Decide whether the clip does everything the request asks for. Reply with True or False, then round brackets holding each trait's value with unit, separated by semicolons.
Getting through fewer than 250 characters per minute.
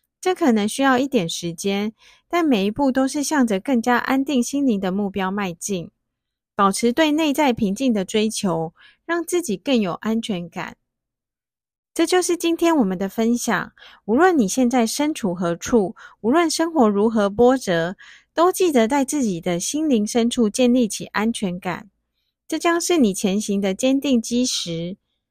True (240 characters per minute)